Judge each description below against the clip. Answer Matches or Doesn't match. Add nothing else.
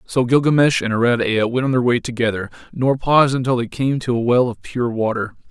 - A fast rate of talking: Matches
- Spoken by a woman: Doesn't match